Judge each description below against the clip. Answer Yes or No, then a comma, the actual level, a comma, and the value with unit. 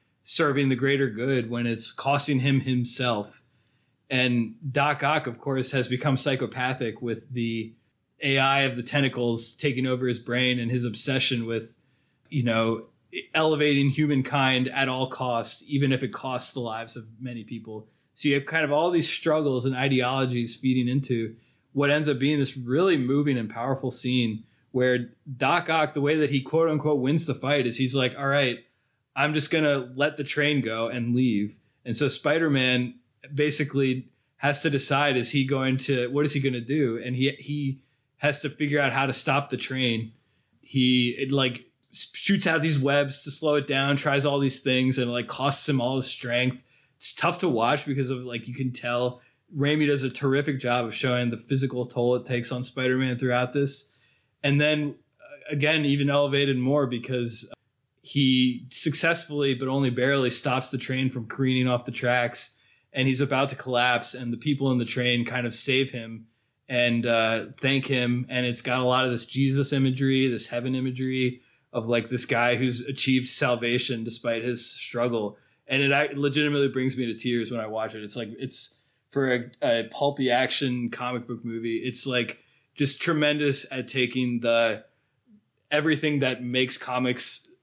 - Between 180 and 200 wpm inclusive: Yes, average, 185 wpm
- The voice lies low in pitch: Yes, low, 130 Hz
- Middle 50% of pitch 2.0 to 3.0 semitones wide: Yes, narrow, 2.4 semitones